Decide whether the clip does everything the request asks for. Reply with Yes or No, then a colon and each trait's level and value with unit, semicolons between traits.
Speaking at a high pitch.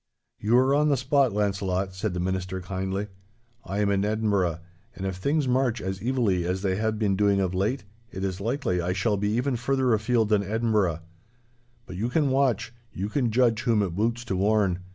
No: low, 105 Hz